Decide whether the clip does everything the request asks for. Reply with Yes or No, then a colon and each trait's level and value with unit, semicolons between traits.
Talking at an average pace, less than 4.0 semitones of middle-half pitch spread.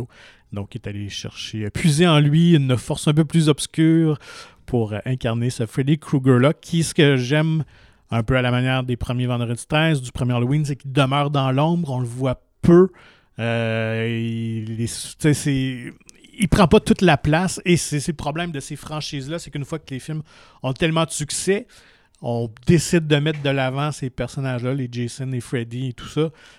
No: average, 190 wpm; average, 4.3 semitones